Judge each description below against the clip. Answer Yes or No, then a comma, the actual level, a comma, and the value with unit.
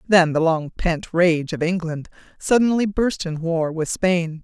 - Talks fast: No, average, 175 wpm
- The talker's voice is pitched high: No, medium, 170 Hz